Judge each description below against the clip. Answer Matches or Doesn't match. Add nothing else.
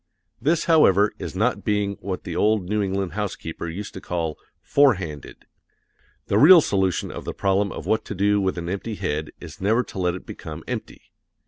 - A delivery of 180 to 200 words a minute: Matches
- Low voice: Matches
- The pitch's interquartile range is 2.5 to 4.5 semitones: Matches